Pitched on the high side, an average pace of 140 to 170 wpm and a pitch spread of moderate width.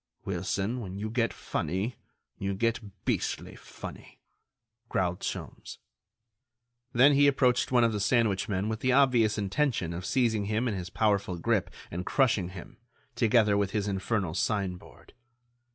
No: low, 105 Hz; average, 150 wpm; average, 3.7 semitones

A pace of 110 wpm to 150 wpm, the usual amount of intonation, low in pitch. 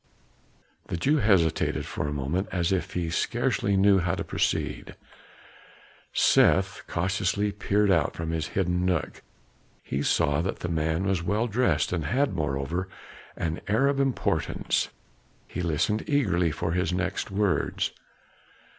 Yes: average, 140 wpm; average, 3.7 semitones; very low, 90 Hz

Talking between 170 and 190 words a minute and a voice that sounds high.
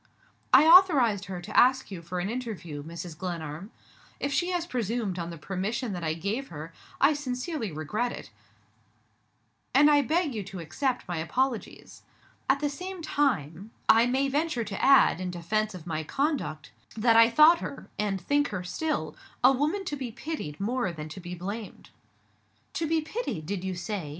Yes: average, 180 wpm; high, 220 Hz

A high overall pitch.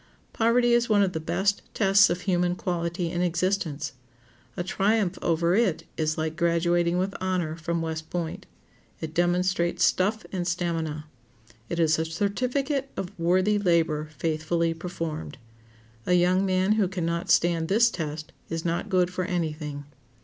No: medium, 175 Hz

